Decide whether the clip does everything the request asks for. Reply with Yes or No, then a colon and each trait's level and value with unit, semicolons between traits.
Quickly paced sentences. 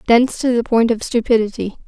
No: average, 190 wpm